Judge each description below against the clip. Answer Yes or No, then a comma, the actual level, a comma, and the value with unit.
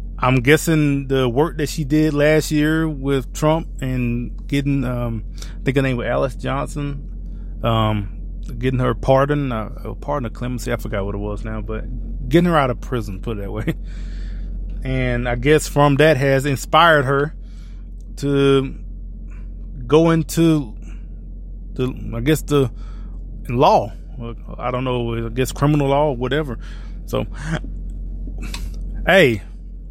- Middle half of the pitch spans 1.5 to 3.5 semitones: No, average, 5.3 semitones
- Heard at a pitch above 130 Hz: No, low, 120 Hz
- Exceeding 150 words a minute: No, average, 145 wpm